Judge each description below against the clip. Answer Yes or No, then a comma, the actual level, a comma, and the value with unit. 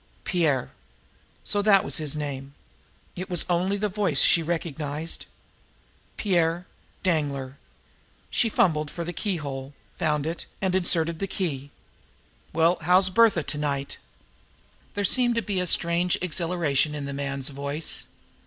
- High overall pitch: No, medium, 165 Hz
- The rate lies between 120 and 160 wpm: Yes, slow, 135 wpm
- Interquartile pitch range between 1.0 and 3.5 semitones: No, average, 4.2 semitones